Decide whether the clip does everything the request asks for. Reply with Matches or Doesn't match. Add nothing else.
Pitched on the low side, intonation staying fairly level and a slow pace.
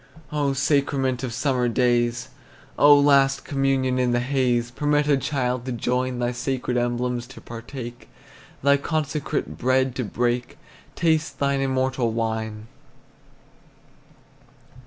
Matches